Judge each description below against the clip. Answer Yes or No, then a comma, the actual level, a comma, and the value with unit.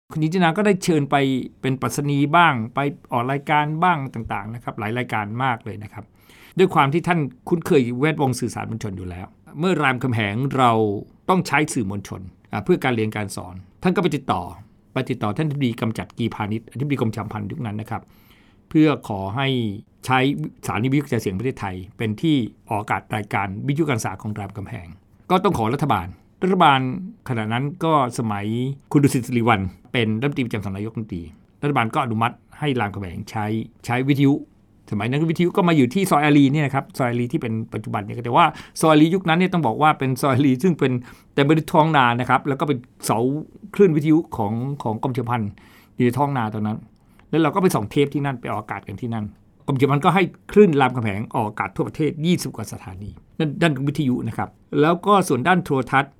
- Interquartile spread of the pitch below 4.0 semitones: No, wide, 5.5 semitones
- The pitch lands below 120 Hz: No, low, 125 Hz